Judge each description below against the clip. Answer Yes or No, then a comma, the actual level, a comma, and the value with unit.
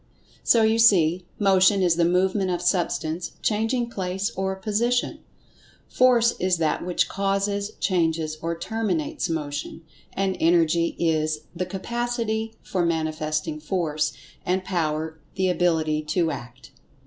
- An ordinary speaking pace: No, slow, 125 wpm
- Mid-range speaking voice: Yes, medium, 180 Hz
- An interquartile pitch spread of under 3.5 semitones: No, average, 3.8 semitones